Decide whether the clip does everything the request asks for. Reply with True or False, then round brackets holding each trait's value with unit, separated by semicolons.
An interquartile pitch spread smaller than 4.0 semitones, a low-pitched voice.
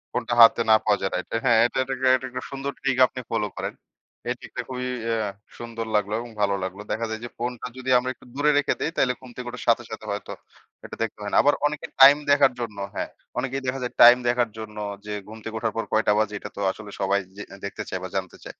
True (3.2 semitones; 120 Hz)